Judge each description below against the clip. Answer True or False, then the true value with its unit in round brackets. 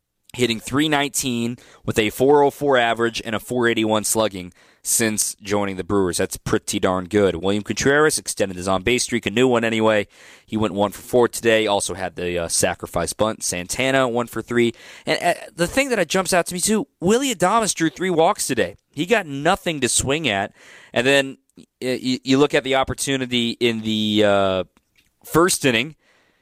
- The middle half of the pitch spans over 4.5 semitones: True (4.9 semitones)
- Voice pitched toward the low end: True (120 Hz)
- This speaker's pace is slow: False (180 wpm)